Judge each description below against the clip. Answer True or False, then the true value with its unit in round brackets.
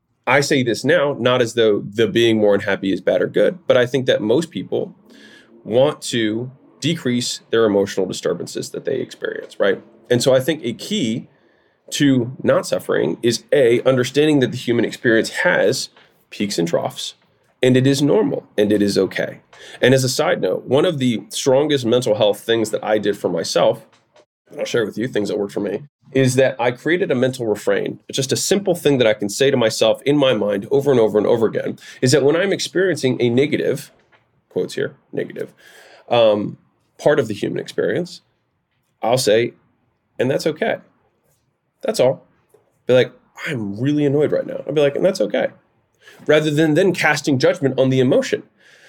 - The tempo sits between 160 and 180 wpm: False (195 wpm)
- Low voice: True (130 Hz)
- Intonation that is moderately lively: True (4.0 semitones)